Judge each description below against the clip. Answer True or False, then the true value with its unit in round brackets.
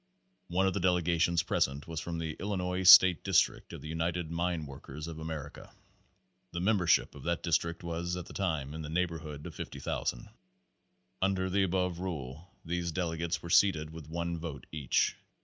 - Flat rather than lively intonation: True (2.2 semitones)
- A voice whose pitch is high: False (85 Hz)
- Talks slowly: False (175 wpm)